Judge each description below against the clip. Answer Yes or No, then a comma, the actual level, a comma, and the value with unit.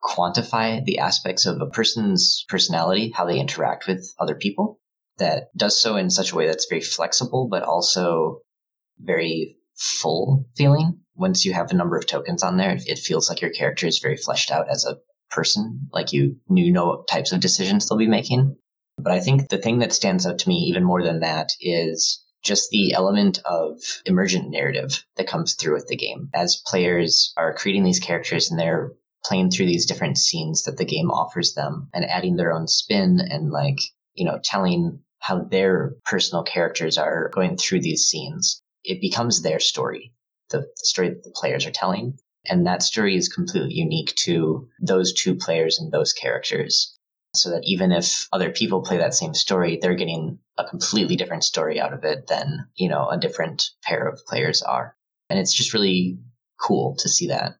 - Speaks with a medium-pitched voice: Yes, medium, 145 Hz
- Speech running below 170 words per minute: No, average, 190 wpm